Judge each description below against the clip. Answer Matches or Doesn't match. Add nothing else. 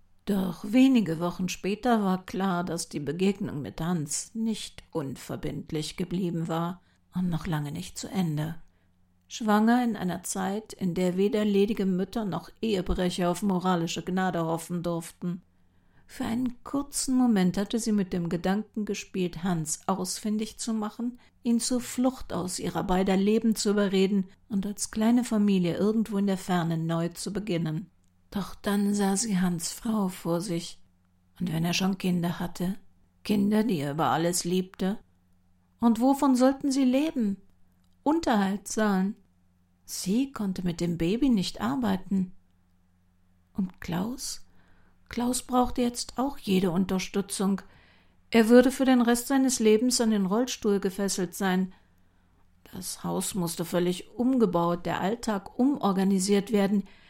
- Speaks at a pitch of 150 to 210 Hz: Matches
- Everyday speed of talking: Matches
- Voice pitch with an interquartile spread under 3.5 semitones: Doesn't match